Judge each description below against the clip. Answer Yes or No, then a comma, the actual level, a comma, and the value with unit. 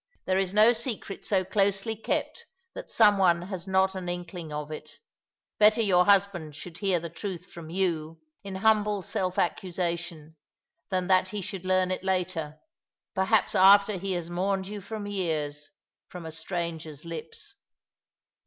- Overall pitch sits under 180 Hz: No, medium, 185 Hz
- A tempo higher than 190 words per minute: No, average, 165 wpm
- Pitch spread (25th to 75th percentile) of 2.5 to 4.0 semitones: Yes, average, 2.8 semitones